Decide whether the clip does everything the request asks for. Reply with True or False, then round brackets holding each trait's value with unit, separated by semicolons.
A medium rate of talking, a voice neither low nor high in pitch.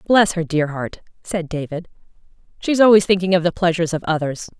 True (195 wpm; 175 Hz)